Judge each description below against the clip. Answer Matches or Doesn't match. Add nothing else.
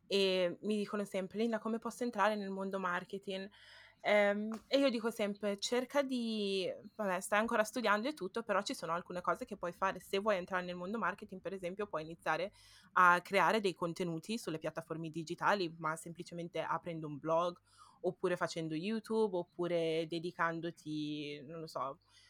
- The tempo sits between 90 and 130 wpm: Doesn't match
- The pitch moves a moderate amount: Matches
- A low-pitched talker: Doesn't match